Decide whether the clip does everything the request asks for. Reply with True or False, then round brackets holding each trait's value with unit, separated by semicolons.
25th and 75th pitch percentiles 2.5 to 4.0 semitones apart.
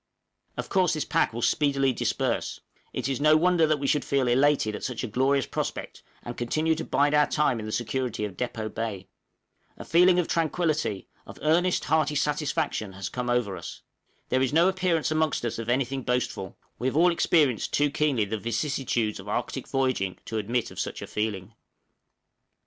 False (5.1 semitones)